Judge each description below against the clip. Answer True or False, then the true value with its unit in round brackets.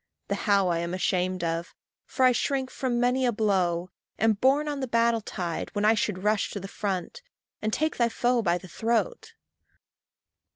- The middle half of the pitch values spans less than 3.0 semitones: False (5.1 semitones)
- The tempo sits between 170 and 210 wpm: True (190 wpm)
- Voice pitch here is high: True (215 Hz)